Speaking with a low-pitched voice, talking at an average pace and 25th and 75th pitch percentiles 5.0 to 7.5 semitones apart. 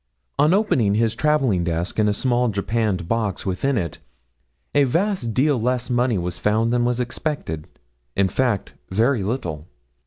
No: low, 115 Hz; average, 155 wpm; average, 4.6 semitones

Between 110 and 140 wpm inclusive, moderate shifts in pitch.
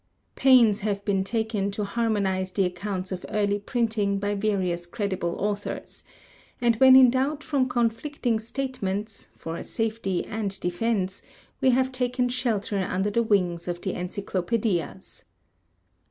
Yes: slow, 135 wpm; average, 3.5 semitones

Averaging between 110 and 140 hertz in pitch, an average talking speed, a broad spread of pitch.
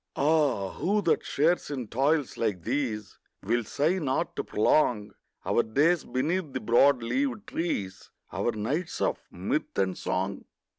Yes: low, 135 Hz; average, 145 wpm; wide, 6.7 semitones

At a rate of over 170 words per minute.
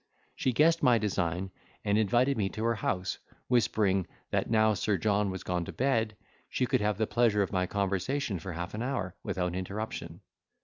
Yes: average, 185 wpm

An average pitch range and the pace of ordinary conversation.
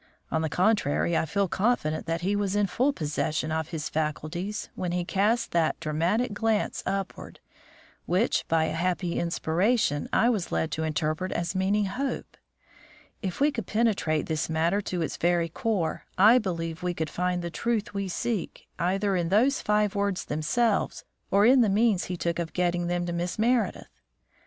Yes: average, 4.1 semitones; average, 175 wpm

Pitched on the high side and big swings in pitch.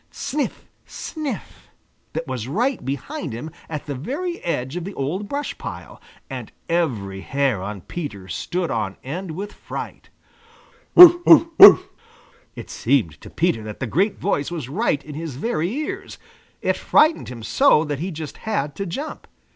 No: medium, 160 Hz; wide, 8.1 semitones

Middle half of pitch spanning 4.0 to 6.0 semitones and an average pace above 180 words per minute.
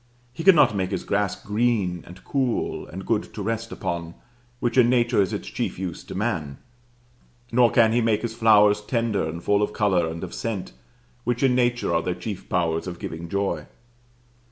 Yes: average, 4.7 semitones; average, 190 wpm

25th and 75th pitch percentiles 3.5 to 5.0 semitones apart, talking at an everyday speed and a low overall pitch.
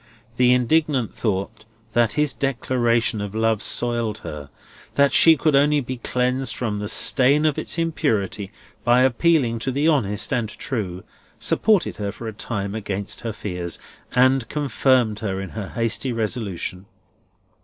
Yes: average, 4.2 semitones; average, 150 wpm; low, 115 Hz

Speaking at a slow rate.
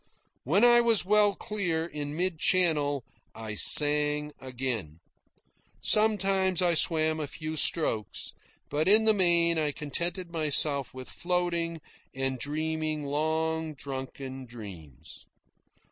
Yes: slow, 115 wpm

